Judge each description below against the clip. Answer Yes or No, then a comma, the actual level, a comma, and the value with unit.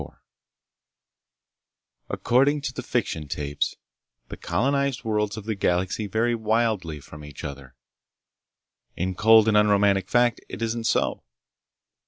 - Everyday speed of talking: No, slow, 125 wpm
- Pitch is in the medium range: No, low, 105 Hz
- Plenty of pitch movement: No, average, 4.8 semitones